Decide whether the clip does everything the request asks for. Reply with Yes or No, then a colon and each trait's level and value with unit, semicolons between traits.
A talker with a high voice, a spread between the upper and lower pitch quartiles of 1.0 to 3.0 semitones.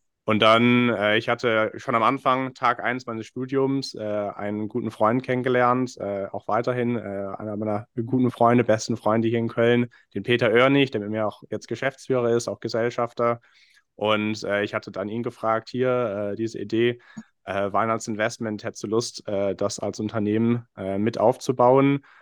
No: low, 115 Hz; narrow, 2.4 semitones